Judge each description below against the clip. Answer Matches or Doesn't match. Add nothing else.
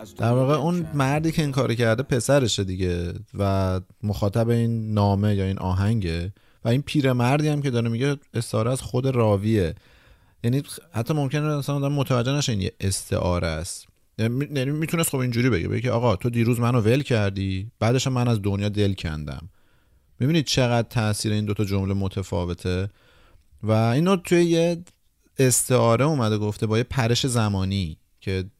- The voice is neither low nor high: Doesn't match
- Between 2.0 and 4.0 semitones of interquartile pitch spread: Doesn't match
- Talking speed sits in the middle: Doesn't match